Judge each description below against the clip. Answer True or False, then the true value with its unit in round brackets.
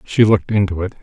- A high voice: False (100 Hz)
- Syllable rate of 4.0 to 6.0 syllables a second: False (7.1 syllables/s)